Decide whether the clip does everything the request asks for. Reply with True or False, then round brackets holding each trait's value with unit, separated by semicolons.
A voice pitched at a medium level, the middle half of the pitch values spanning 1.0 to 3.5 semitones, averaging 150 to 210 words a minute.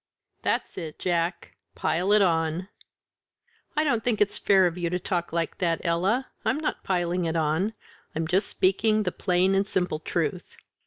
True (180 Hz; 3.0 semitones; 170 wpm)